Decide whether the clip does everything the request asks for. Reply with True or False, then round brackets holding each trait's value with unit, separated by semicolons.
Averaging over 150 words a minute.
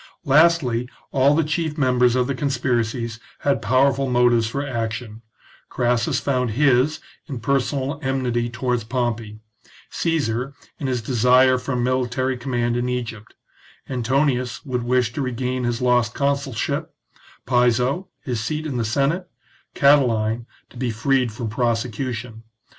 False (135 wpm)